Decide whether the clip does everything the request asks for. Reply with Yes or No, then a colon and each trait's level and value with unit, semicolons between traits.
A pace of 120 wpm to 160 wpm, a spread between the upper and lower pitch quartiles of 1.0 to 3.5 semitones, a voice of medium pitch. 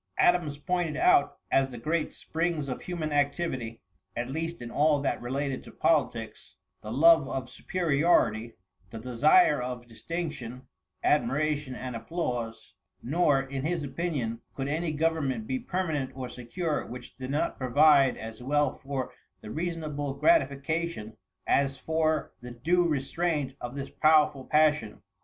No: average, 140 wpm; average, 4.2 semitones; medium, 145 Hz